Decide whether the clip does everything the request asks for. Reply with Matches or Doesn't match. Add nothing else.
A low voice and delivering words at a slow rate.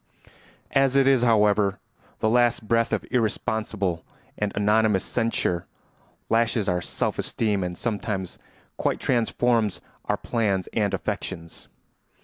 Matches